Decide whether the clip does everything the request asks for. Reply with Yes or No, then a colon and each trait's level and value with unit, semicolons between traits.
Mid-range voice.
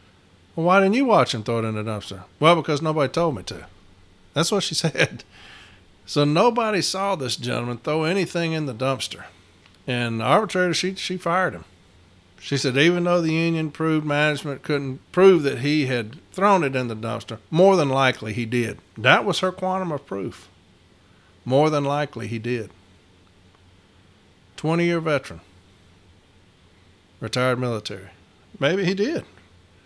No: low, 125 Hz